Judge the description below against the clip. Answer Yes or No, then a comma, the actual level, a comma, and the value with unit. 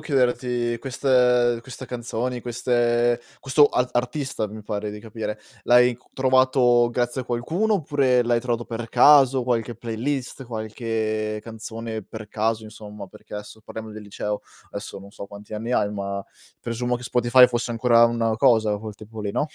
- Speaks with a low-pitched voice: Yes, low, 120 Hz